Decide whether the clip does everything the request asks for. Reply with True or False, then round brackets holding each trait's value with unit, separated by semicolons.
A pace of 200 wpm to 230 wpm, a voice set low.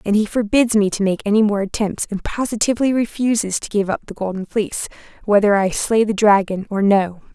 False (205 wpm; 210 Hz)